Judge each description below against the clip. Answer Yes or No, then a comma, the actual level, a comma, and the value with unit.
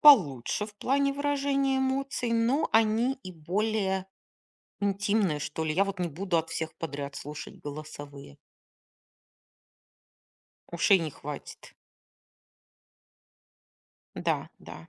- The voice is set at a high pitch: Yes, high, 195 Hz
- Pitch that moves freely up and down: Yes, wide, 7.4 semitones